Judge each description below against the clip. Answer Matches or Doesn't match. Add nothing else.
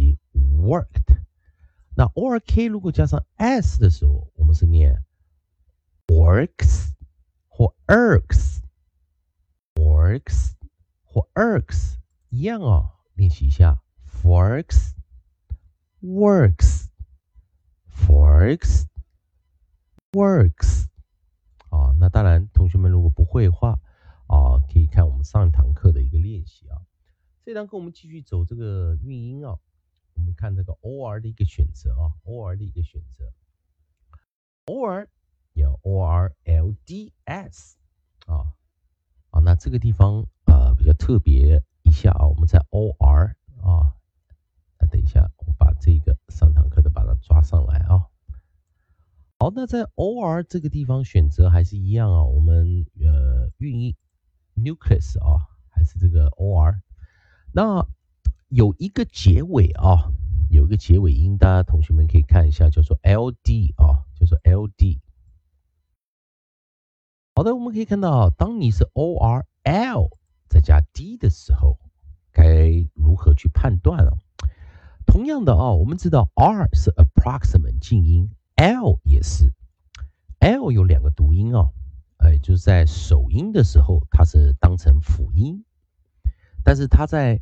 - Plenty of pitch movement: Doesn't match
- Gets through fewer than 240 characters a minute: Matches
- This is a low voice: Matches